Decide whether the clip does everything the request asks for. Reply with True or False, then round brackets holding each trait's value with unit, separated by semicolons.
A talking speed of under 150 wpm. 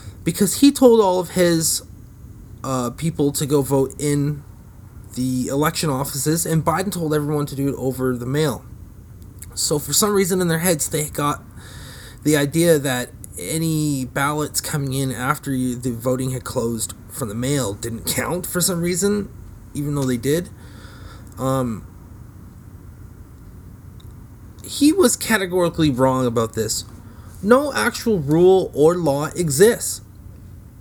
True (140 wpm)